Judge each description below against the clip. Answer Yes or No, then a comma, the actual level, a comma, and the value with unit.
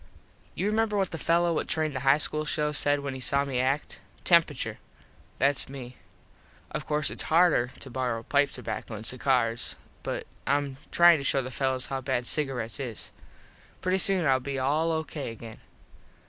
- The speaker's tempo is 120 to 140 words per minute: No, average, 175 wpm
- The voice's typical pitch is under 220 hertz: Yes, medium, 140 Hz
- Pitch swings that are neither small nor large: Yes, average, 3.3 semitones